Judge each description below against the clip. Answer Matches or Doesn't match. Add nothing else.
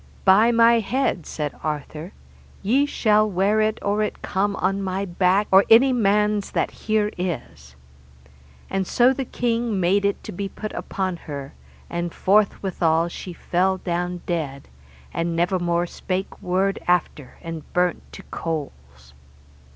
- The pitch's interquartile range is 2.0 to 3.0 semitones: Doesn't match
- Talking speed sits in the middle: Matches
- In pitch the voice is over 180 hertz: Matches